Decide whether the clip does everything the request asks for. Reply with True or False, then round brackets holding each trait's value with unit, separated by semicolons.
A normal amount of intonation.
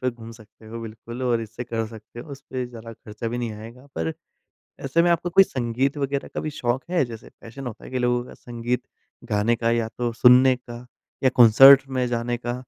False (2.1 semitones)